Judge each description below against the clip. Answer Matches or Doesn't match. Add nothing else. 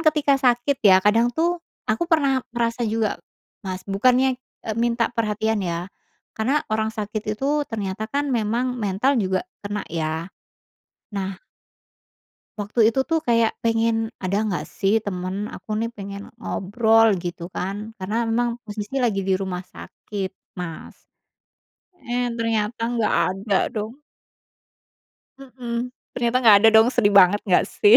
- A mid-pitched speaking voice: Doesn't match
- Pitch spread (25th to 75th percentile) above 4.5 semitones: Doesn't match